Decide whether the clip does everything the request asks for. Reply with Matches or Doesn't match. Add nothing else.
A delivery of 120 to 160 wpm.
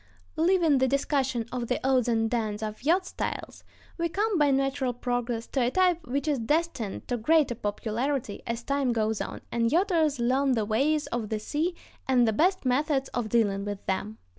Doesn't match